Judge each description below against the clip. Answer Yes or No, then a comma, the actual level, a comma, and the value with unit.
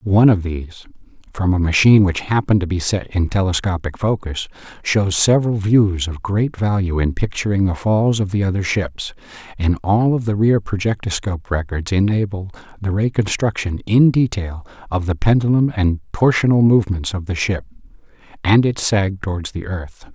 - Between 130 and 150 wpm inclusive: No, average, 165 wpm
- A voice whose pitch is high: No, low, 100 Hz